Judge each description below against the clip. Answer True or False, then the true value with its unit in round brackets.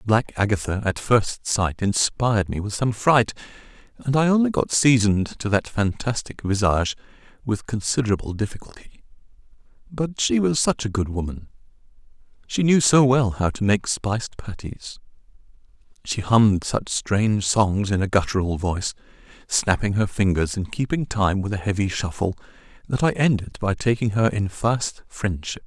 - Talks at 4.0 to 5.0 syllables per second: True (4.9 syllables/s)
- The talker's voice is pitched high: False (110 Hz)